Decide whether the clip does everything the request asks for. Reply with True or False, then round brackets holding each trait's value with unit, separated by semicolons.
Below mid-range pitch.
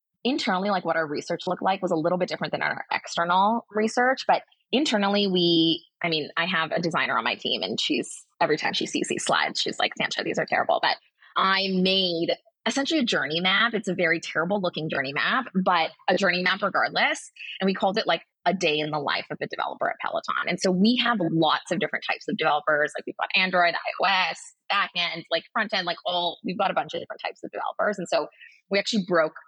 False (180 Hz)